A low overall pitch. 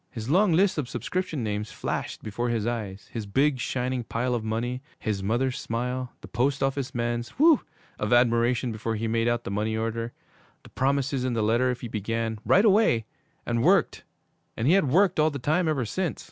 Yes: low, 120 Hz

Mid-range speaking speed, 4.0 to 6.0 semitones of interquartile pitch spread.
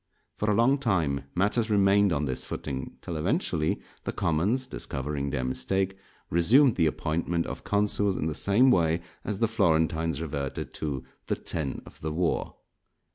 Yes: average, 160 wpm; average, 5.1 semitones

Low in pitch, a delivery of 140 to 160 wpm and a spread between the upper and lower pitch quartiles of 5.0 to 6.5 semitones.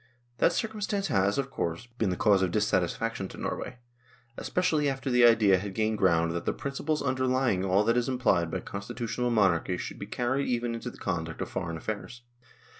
No: low, 115 Hz; average, 195 wpm; average, 5.3 semitones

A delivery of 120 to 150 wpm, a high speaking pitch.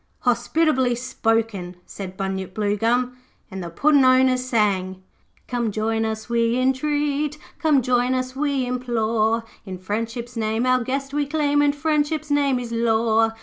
Yes: average, 145 wpm; high, 245 Hz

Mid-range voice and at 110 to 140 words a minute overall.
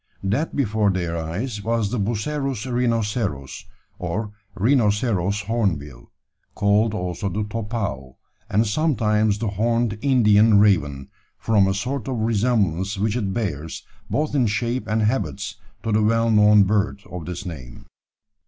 No: low, 105 Hz; slow, 135 wpm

